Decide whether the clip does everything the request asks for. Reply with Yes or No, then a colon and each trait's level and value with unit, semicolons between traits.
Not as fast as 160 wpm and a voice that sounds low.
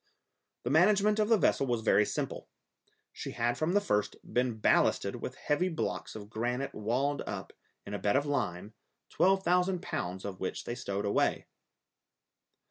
No: average, 165 wpm; low, 125 Hz